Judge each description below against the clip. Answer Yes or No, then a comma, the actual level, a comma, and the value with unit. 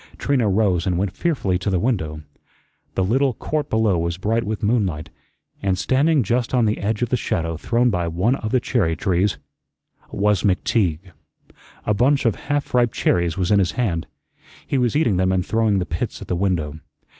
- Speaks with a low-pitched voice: Yes, low, 100 Hz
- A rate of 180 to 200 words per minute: Yes, average, 190 wpm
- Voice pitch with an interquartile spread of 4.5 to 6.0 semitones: Yes, average, 5.1 semitones